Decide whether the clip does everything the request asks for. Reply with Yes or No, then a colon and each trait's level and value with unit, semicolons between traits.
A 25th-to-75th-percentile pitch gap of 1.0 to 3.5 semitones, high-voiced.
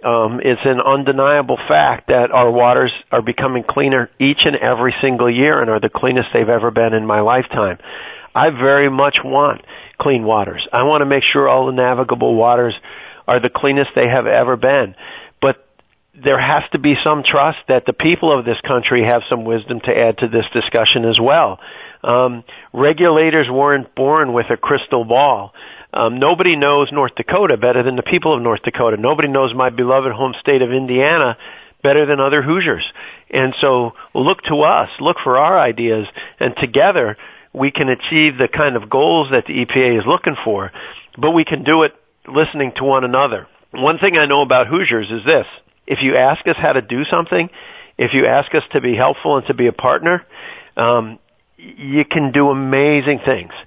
No: average, 3.0 semitones; low, 130 Hz